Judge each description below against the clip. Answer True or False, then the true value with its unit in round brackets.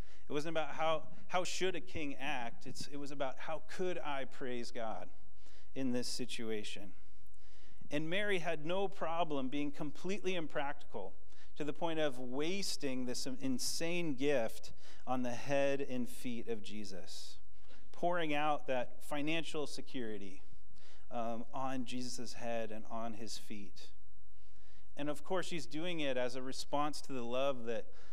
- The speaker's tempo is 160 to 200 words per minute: False (150 wpm)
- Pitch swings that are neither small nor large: False (5.9 semitones)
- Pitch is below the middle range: True (130 Hz)